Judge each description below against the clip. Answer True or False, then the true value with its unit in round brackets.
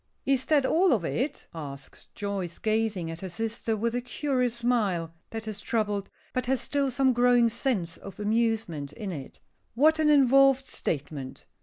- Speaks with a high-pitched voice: True (225 Hz)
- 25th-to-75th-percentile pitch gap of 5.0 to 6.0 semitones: True (5.4 semitones)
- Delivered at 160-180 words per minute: True (165 wpm)